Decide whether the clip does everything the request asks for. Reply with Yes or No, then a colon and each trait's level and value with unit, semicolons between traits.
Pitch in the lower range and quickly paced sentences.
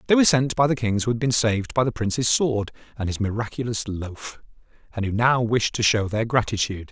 Yes: low, 115 Hz; fast, 225 wpm